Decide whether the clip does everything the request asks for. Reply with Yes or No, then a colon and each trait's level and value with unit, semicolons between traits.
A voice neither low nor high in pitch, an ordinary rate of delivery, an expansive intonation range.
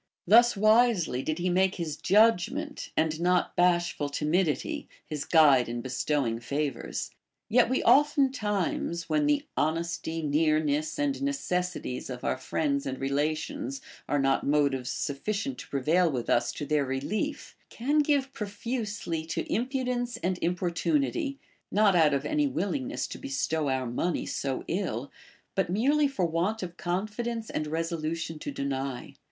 Yes: medium, 170 Hz; average, 145 wpm; wide, 7.8 semitones